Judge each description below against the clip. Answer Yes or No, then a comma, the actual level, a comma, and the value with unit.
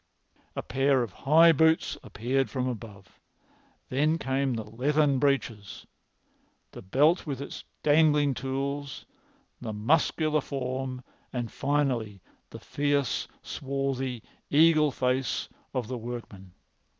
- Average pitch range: Yes, average, 3.0 semitones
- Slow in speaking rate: Yes, slow, 115 wpm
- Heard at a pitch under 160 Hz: Yes, low, 135 Hz